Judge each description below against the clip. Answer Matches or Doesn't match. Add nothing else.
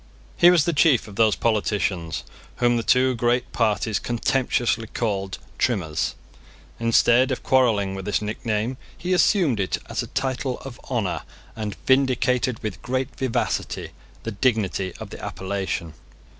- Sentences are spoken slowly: Doesn't match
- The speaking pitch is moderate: Doesn't match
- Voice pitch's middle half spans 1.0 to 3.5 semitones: Doesn't match